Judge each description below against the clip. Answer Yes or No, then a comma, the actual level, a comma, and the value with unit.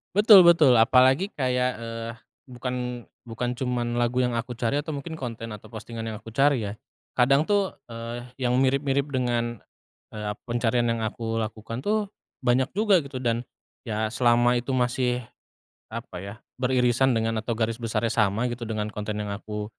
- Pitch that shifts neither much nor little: No, narrow, 2.3 semitones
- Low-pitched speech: Yes, low, 120 Hz